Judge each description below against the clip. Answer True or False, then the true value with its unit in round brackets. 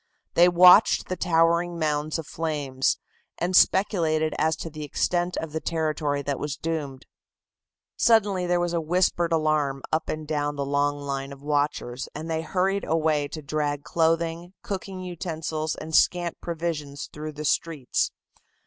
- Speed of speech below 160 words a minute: True (150 wpm)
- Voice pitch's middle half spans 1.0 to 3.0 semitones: True (2.7 semitones)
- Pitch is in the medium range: True (160 Hz)